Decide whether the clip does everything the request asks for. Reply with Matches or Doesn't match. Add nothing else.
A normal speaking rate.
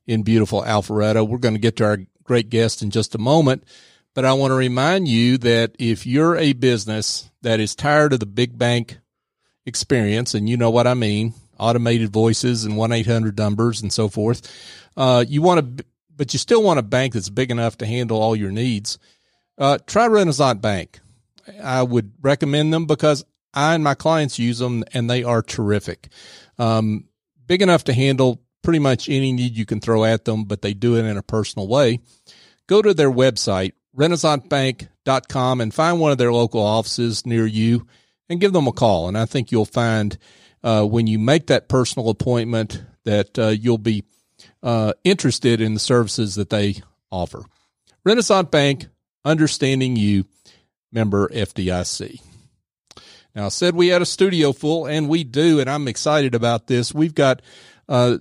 Matches